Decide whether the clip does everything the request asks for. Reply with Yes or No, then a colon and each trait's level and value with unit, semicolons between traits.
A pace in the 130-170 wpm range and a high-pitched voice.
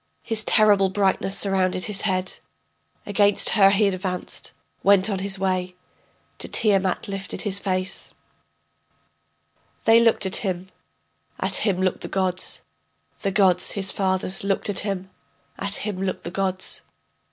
Yes: average, 140 wpm; high, 195 Hz